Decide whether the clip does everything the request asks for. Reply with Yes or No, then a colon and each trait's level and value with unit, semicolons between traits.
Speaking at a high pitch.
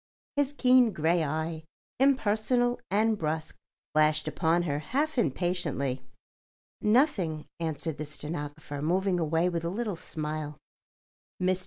No: medium, 170 Hz